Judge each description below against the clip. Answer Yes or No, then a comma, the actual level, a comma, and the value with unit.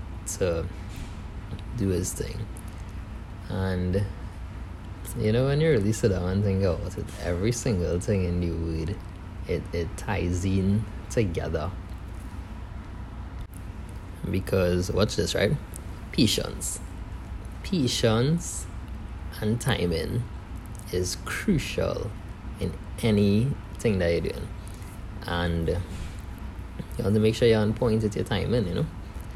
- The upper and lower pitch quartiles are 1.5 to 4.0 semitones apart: Yes, average, 2.8 semitones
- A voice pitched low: Yes, very low, 95 Hz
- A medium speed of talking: No, slow, 115 wpm